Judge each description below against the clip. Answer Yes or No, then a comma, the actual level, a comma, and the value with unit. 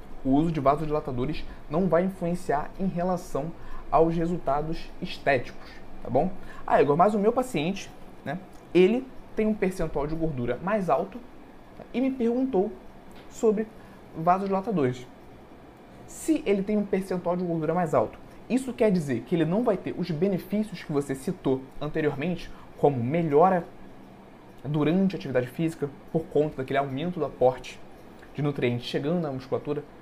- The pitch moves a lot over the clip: No, average, 5.0 semitones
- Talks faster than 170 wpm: No, average, 150 wpm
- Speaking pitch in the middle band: Yes, medium, 165 Hz